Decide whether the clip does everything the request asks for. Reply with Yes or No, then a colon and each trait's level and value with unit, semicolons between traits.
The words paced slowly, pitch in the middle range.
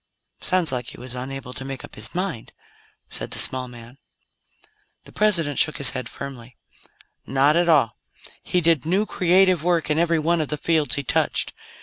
No: average, 185 wpm; medium, 150 Hz